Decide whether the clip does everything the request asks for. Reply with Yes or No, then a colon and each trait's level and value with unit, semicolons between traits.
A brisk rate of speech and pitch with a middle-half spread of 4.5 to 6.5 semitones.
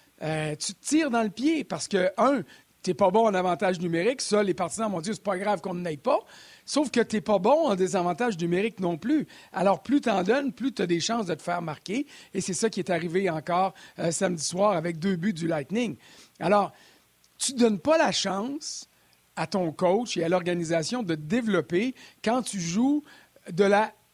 Yes: fast, 225 wpm; average, 4.8 semitones